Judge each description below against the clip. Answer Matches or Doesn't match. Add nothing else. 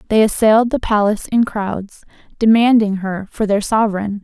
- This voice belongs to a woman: Matches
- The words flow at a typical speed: Matches